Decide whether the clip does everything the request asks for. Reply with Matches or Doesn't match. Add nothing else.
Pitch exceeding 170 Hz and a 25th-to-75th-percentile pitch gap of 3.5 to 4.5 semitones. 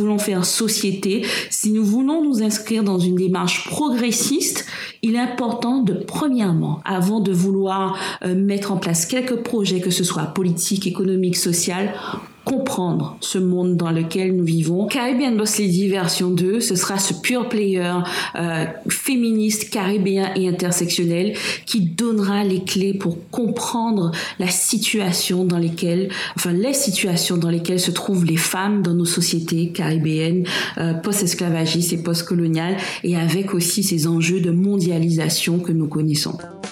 Doesn't match